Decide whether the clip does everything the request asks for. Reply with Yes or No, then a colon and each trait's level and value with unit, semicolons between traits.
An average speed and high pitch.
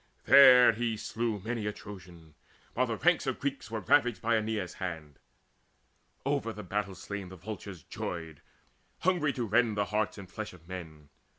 No: average, 170 wpm; low, 105 Hz